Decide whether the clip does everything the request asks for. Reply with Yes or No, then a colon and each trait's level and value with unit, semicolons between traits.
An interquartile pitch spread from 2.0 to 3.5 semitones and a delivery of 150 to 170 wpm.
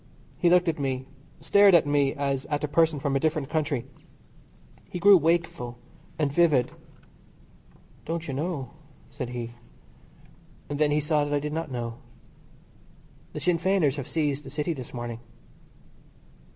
Yes: average, 3.2 semitones; average, 155 wpm